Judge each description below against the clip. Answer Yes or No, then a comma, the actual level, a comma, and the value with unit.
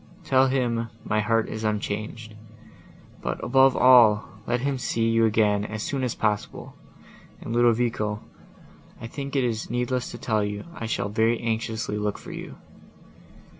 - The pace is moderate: Yes, average, 155 wpm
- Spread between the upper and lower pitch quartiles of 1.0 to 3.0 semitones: Yes, narrow, 2.4 semitones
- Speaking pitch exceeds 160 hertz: No, low, 115 Hz